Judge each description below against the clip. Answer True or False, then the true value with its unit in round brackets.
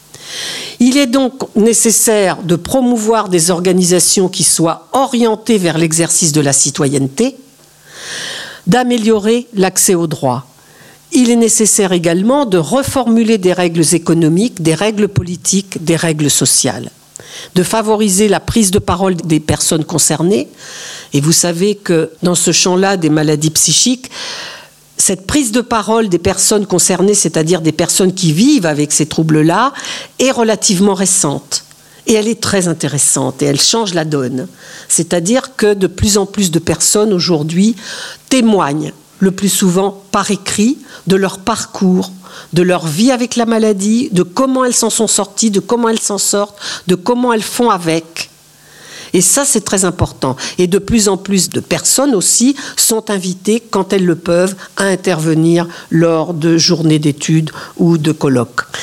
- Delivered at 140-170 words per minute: True (155 wpm)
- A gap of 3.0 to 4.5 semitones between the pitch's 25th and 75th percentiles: False (5.1 semitones)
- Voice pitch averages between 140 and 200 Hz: True (190 Hz)